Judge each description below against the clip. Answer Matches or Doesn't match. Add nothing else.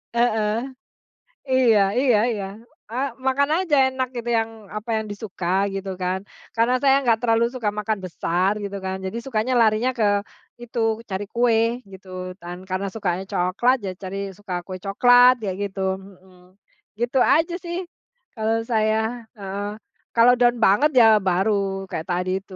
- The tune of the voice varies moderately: Matches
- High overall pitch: Matches